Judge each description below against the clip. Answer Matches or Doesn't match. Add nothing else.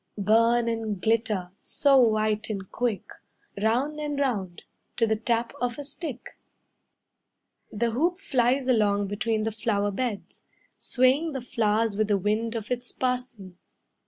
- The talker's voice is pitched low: Doesn't match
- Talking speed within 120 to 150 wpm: Matches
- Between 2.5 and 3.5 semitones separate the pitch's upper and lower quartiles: Matches